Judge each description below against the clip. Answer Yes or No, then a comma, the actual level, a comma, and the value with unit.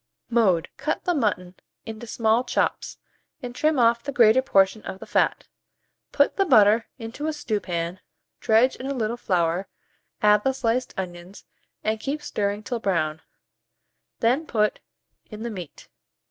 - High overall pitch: Yes, high, 220 Hz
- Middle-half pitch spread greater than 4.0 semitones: Yes, average, 4.5 semitones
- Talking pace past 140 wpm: Yes, average, 150 wpm